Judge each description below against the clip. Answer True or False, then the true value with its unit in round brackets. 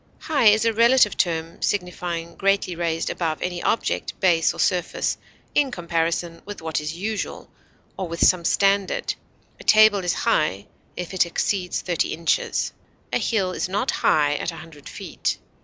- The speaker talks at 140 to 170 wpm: True (160 wpm)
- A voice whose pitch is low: False (180 Hz)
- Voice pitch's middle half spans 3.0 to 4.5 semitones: True (3.4 semitones)